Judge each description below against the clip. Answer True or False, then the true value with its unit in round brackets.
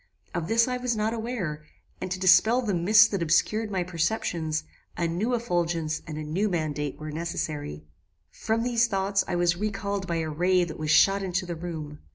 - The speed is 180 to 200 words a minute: True (195 wpm)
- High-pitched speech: False (180 Hz)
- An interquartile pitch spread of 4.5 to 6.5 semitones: True (5.0 semitones)